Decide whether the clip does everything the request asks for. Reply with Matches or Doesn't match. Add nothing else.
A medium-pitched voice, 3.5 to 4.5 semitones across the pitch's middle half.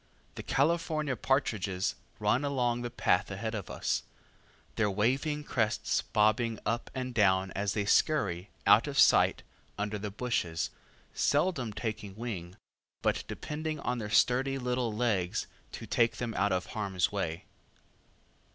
Doesn't match